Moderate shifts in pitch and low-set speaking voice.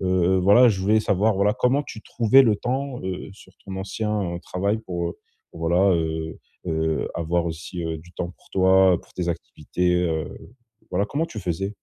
Yes: average, 3.4 semitones; very low, 95 Hz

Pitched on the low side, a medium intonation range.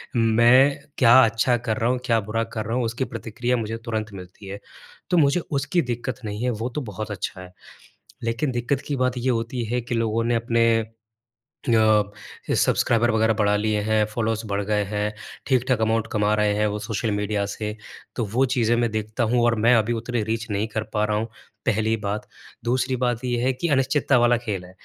No: low, 115 Hz; narrow, 2.3 semitones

